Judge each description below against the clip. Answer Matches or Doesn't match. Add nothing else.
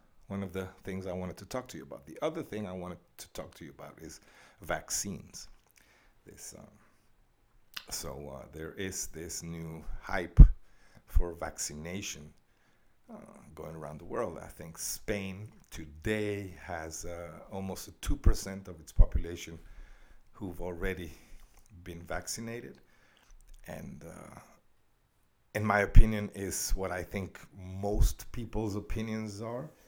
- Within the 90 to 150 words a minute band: Matches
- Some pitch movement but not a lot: Matches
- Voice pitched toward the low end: Matches